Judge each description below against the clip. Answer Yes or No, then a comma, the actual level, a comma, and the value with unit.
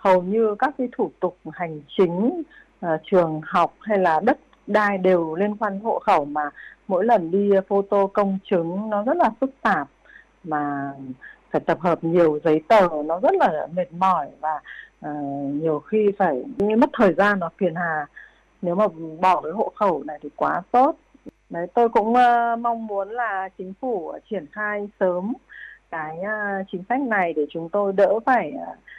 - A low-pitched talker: No, high, 190 Hz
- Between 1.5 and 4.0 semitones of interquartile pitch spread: No, average, 4.5 semitones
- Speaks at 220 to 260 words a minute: No, average, 185 wpm